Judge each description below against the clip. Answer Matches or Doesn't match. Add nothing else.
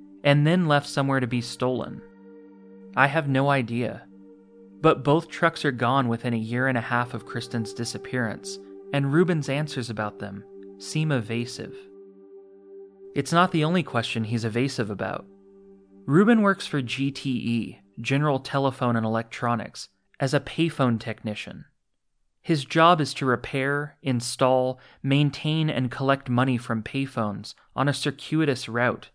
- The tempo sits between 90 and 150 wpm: Matches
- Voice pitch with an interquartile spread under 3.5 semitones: Doesn't match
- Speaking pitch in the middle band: Doesn't match